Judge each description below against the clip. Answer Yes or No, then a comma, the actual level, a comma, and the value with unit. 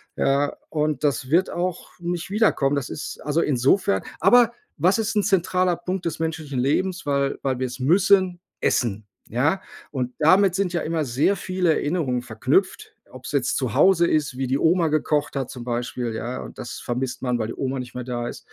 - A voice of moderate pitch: Yes, medium, 150 Hz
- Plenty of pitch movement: Yes, wide, 6.1 semitones